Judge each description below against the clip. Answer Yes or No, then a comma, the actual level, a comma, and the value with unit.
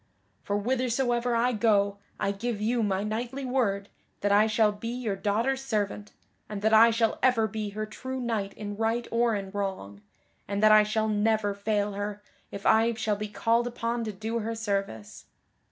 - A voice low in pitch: No, high, 215 Hz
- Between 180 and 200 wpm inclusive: Yes, average, 185 wpm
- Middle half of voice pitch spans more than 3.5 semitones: No, narrow, 2.4 semitones